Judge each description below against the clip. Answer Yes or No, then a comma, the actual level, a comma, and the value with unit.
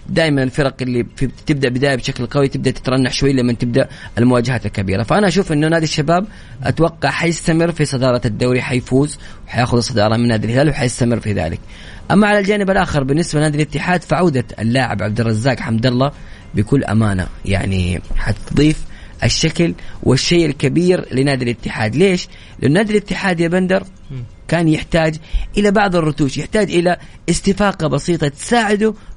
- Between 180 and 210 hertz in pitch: No, low, 135 Hz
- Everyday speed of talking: No, fast, 150 wpm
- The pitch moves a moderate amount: No, wide, 6.0 semitones